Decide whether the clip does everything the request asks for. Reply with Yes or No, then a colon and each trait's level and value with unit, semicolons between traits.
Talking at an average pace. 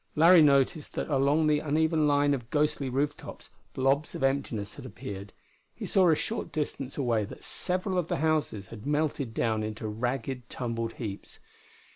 Yes: average, 170 wpm